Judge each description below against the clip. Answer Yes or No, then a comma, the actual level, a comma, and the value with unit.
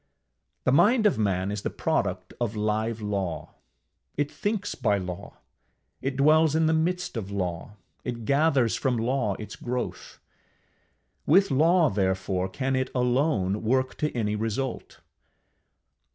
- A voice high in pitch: No, low, 120 Hz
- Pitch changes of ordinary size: No, wide, 6.1 semitones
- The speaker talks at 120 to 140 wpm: Yes, slow, 135 wpm